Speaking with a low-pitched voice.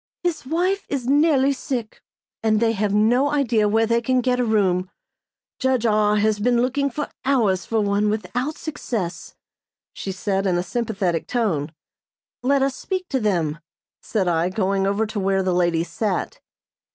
No: high, 220 Hz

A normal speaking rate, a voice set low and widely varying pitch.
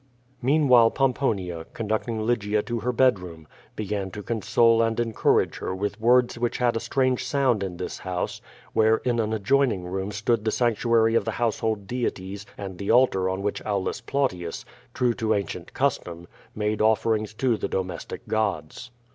No: average, 165 wpm; low, 110 Hz; average, 3.4 semitones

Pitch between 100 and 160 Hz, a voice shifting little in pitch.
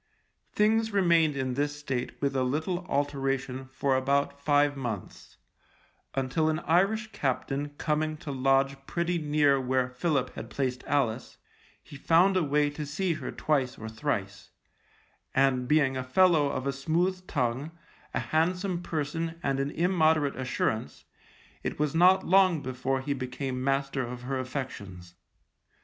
No: medium, 140 Hz; average, 3.6 semitones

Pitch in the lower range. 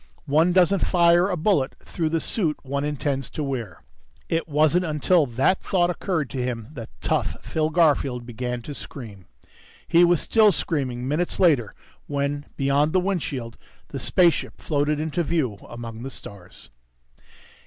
No: medium, 150 Hz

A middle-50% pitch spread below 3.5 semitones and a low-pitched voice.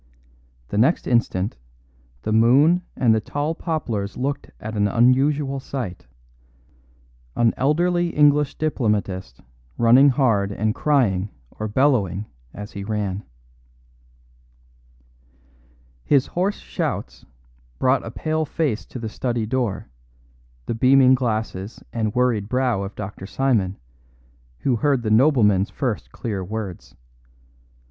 No: average, 4.8 semitones; low, 120 Hz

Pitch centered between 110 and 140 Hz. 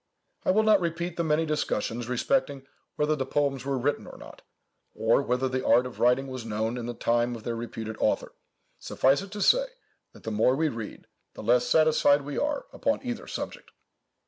Yes: low, 135 Hz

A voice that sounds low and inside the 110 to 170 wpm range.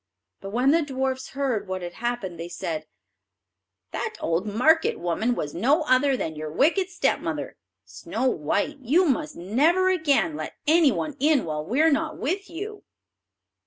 No: very high, 260 Hz; average, 160 wpm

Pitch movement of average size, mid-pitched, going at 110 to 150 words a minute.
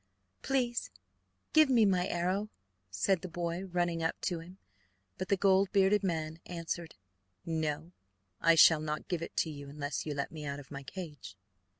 No: average, 3.7 semitones; medium, 170 Hz; average, 175 wpm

